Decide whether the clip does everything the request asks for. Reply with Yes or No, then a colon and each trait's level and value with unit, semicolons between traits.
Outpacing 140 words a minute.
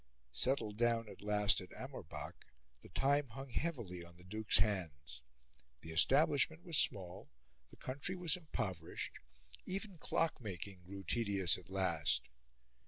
No: slow, 135 wpm